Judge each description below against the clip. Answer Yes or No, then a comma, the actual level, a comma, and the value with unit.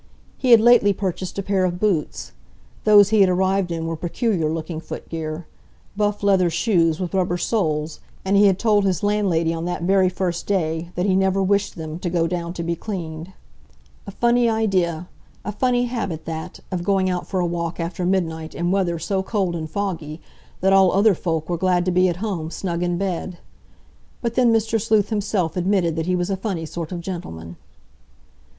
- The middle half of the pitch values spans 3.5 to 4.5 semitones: No, average, 3.0 semitones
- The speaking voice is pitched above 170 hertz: Yes, medium, 185 Hz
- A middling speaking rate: Yes, average, 195 wpm